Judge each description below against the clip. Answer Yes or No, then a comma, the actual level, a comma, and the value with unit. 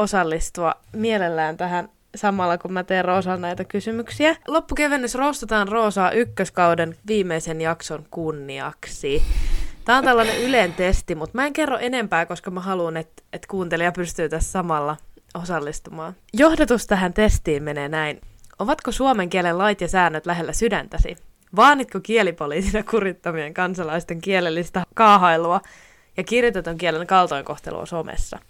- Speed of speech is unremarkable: Yes, average, 130 wpm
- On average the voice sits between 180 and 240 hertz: Yes, medium, 185 Hz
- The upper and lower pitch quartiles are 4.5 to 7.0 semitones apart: Yes, average, 5.1 semitones